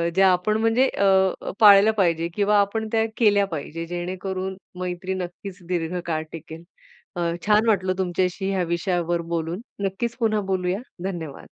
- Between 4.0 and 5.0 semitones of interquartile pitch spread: No, narrow, 2.6 semitones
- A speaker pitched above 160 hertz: Yes, high, 190 Hz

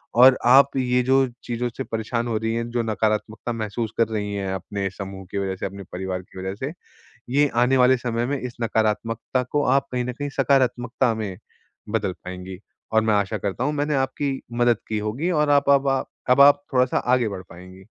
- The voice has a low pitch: Yes, low, 115 Hz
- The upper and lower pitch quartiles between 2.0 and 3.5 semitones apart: No, average, 4.2 semitones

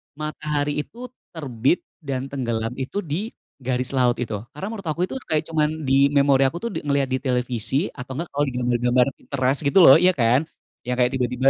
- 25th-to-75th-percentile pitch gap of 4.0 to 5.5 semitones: No, average, 3.4 semitones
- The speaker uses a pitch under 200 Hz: Yes, low, 135 Hz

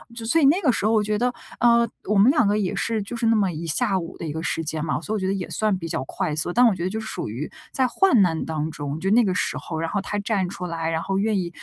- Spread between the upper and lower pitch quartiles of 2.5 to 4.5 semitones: No, average, 5.2 semitones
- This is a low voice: No, high, 195 Hz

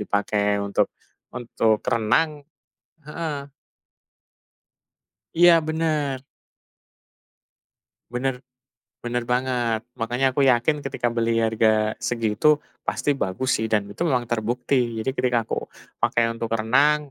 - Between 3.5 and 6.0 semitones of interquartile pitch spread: Yes, average, 3.9 semitones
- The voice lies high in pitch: No, low, 120 Hz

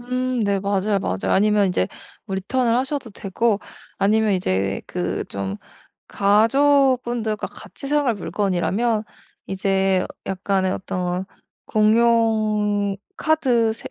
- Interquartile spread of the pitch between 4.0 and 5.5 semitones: No, average, 3.6 semitones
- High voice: Yes, high, 210 Hz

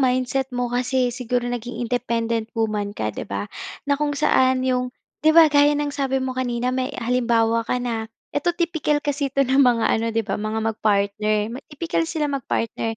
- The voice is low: No, very high, 250 Hz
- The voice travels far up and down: No, average, 3.4 semitones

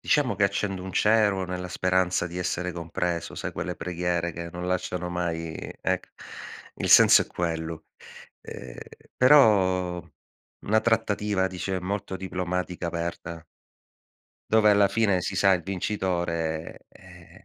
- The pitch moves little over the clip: Yes, narrow, 2.2 semitones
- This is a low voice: Yes, very low, 90 Hz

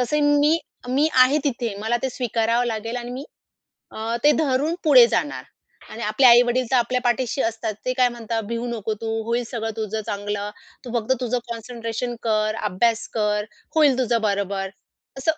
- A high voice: Yes, high, 235 Hz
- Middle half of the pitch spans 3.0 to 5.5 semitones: No, narrow, 2.5 semitones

